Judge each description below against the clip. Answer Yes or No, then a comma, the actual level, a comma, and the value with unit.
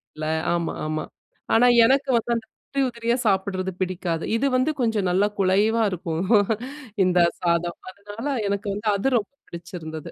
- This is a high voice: Yes, high, 195 Hz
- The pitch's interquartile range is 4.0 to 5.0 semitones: Yes, average, 4.6 semitones